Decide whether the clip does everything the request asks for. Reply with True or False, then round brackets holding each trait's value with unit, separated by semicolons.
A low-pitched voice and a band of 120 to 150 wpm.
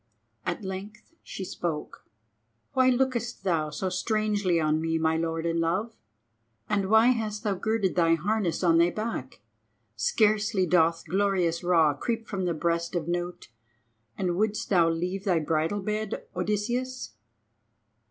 False (185 Hz; 145 wpm)